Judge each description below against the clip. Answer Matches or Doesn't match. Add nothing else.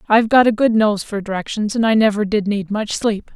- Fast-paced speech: Matches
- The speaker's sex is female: Matches